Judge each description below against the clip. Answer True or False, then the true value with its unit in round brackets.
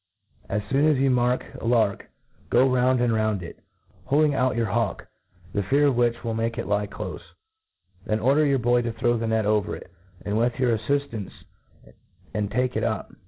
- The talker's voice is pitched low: True (120 Hz)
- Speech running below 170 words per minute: False (190 wpm)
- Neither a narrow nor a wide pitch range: True (3.0 semitones)